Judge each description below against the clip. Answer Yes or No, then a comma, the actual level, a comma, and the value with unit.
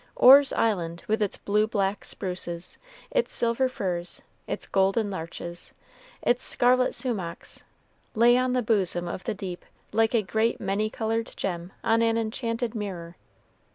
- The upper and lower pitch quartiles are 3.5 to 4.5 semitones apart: Yes, average, 4.0 semitones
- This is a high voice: Yes, high, 215 Hz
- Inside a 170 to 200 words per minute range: No, average, 145 wpm